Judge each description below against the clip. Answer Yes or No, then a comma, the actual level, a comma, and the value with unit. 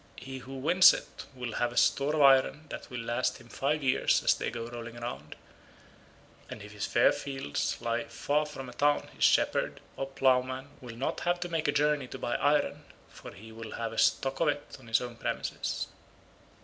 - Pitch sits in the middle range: No, low, 130 Hz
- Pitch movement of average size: Yes, average, 3.4 semitones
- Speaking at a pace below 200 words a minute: No, fast, 205 wpm